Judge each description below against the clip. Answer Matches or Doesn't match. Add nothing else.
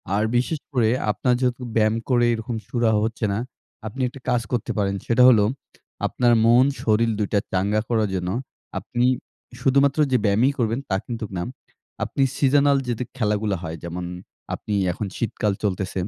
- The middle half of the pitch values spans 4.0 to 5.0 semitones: Doesn't match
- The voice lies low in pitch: Matches